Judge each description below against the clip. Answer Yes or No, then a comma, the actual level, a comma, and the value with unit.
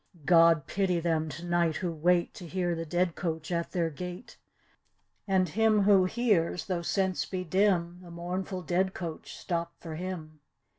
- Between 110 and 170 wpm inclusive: Yes, average, 165 wpm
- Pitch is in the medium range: Yes, medium, 175 Hz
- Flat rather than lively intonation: Yes, narrow, 1.9 semitones